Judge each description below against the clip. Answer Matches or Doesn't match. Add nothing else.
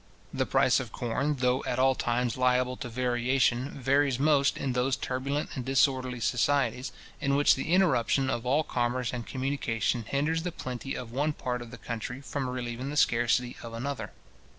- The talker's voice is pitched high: Doesn't match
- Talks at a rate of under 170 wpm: Doesn't match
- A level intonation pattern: Matches